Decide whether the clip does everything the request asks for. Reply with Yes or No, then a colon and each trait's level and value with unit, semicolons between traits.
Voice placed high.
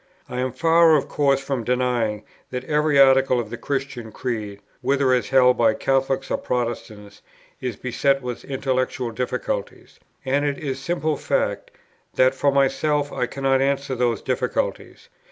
No: low, 130 Hz